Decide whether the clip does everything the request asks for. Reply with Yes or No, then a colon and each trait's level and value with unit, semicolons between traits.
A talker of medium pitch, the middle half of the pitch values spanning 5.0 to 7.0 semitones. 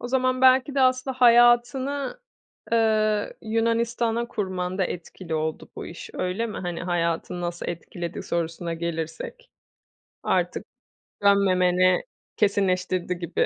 No: high, 200 Hz; wide, 5.4 semitones